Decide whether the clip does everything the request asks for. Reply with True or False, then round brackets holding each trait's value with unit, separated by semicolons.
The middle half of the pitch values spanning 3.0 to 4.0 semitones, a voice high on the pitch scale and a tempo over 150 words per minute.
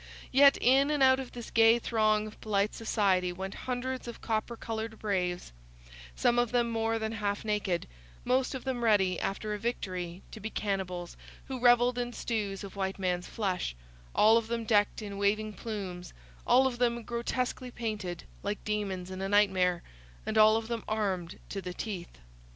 True (3.4 semitones; 215 Hz; 180 wpm)